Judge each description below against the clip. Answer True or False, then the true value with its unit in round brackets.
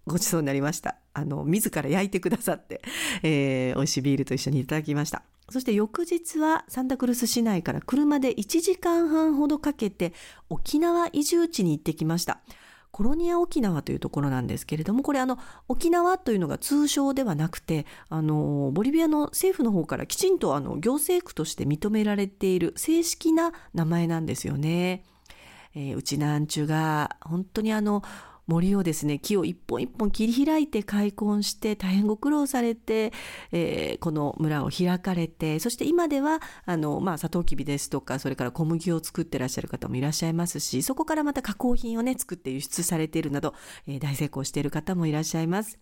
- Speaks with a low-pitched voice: False (190 Hz)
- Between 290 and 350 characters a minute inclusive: False (395 characters per minute)